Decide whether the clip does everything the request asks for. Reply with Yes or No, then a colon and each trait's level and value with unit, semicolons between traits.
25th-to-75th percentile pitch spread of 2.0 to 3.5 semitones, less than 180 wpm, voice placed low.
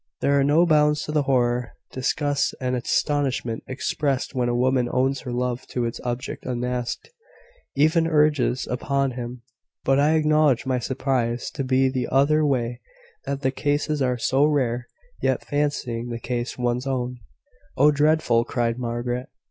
Yes: average, 2.9 semitones; average, 165 wpm; low, 130 Hz